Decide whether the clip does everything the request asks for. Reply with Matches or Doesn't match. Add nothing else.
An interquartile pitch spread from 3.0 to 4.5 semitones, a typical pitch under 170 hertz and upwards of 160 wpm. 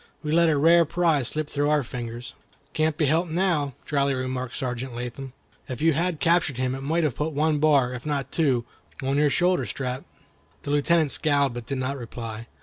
Matches